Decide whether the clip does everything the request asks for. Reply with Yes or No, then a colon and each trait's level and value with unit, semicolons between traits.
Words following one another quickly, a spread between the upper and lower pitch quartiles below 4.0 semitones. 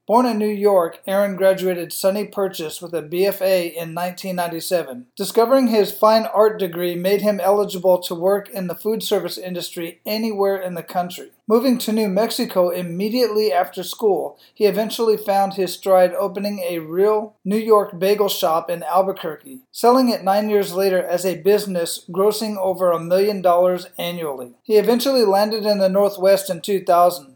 No: average, 165 wpm; average, 2.9 semitones